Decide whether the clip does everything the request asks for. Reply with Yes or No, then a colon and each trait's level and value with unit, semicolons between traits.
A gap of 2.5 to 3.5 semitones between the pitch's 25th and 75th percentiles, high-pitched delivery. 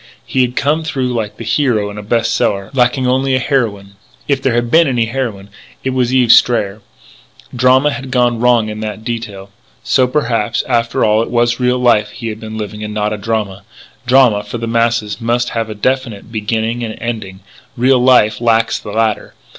No: average, 2.8 semitones; low, 115 Hz